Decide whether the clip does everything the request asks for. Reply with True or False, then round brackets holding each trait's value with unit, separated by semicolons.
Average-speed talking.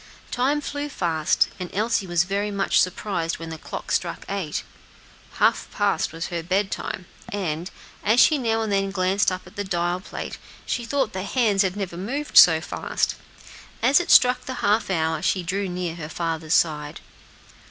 True (175 wpm)